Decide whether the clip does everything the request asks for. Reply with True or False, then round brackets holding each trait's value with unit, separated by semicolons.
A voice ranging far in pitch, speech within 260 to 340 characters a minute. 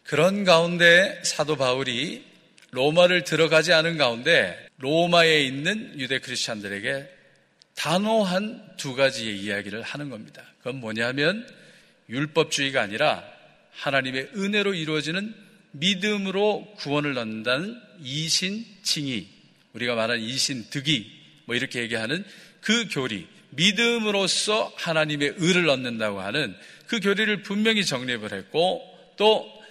True (7.2 semitones; 290 characters per minute)